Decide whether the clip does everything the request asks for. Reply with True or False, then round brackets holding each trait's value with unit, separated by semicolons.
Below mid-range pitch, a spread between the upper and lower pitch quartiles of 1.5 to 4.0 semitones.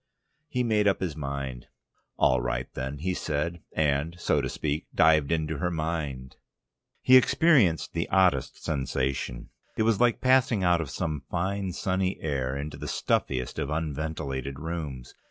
False (80 Hz; 5.0 semitones)